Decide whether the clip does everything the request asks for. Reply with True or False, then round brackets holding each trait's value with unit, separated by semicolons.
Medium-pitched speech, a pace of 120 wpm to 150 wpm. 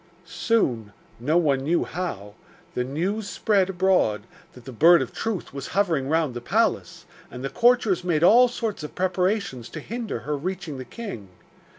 False (170 Hz; 170 wpm)